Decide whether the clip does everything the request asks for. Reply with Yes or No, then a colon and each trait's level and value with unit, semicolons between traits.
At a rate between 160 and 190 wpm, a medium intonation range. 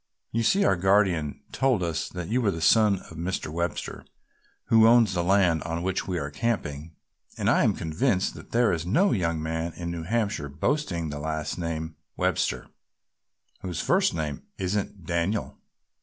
Yes: average, 175 wpm; average, 4.4 semitones